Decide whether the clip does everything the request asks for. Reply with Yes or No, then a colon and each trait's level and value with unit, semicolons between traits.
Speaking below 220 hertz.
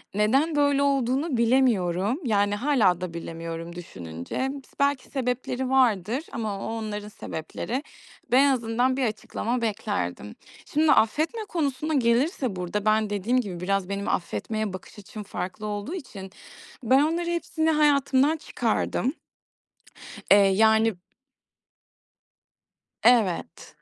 No: high, 230 Hz